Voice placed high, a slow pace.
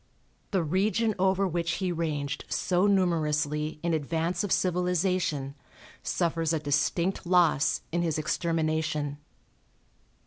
No: medium, 170 Hz; slow, 110 wpm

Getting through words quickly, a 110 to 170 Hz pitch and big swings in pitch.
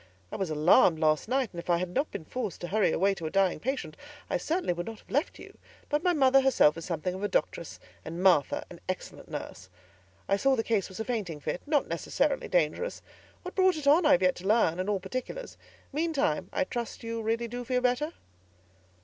No: fast, 225 wpm; high, 220 Hz; wide, 7.4 semitones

